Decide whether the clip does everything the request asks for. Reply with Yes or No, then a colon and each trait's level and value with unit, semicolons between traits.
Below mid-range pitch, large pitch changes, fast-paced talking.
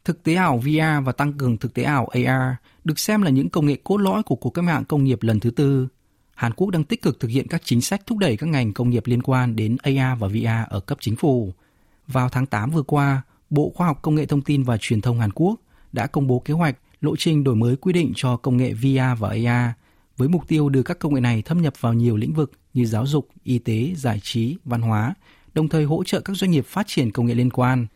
No: low, 130 Hz; average, 4.3 semitones; fast, 265 wpm